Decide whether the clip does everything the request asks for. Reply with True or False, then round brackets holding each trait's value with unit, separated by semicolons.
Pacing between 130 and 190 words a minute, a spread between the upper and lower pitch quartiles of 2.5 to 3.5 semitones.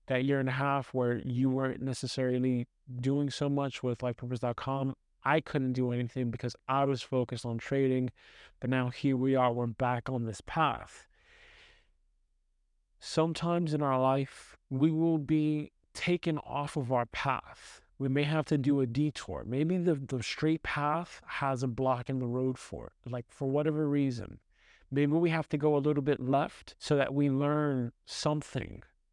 True (175 wpm; 2.9 semitones)